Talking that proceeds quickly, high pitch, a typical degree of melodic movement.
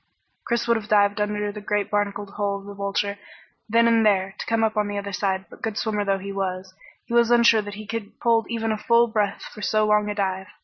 No: fast, 250 wpm; high, 210 Hz; narrow, 1.9 semitones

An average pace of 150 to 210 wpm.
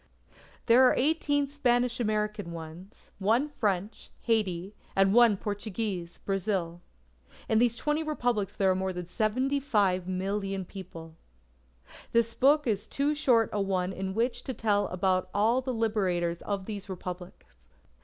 No: slow, 135 wpm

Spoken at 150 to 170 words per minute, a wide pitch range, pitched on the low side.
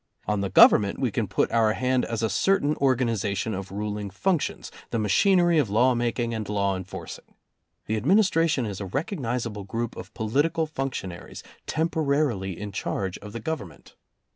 Yes: average, 165 wpm; wide, 5.7 semitones; low, 115 Hz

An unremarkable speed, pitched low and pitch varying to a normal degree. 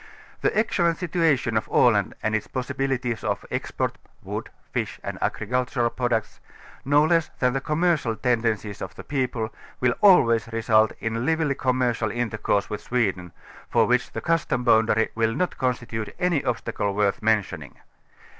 Yes: average, 155 wpm; low, 120 Hz; average, 3.8 semitones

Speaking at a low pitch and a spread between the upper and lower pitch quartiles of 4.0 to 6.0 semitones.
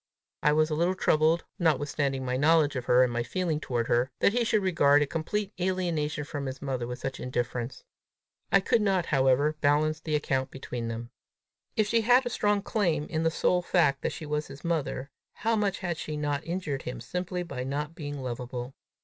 No: medium, 150 Hz; average, 4.9 semitones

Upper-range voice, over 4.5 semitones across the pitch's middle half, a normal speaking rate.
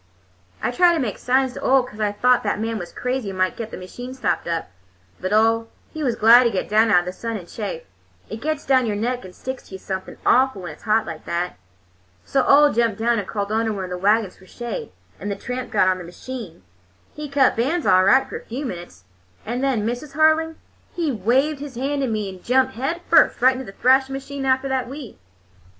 No: high, 235 Hz; average, 5.0 semitones; fast, 235 wpm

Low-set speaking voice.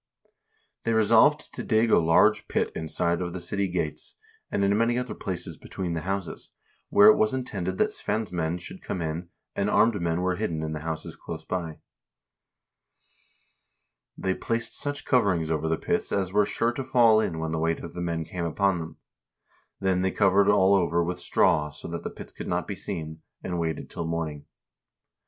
Yes: very low, 90 Hz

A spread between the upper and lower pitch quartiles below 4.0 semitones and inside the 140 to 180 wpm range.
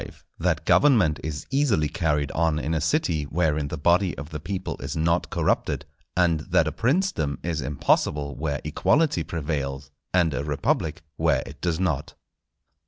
Yes: average, 3.3 semitones; average, 160 wpm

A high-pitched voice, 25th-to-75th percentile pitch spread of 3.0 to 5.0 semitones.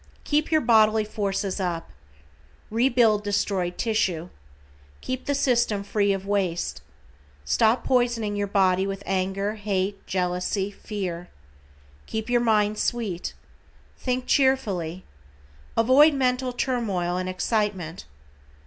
Yes: high, 205 Hz; average, 4.1 semitones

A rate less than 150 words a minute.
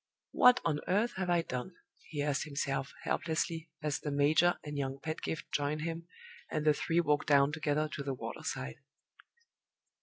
No: average, 170 wpm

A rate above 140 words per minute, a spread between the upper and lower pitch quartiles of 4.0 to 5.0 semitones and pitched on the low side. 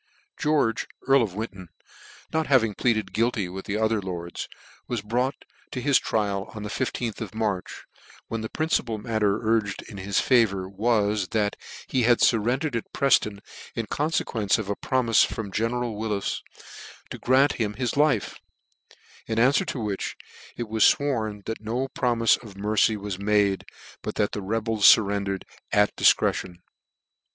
No: average, 160 wpm; average, 2.8 semitones; low, 110 Hz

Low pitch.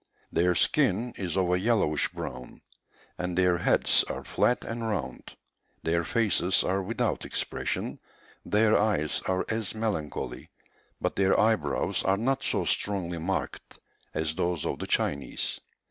Yes: very low, 95 Hz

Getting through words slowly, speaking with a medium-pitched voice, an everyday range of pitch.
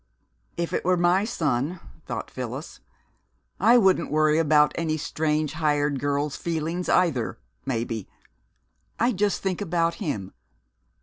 Yes: slow, 125 wpm; medium, 155 Hz; average, 3.5 semitones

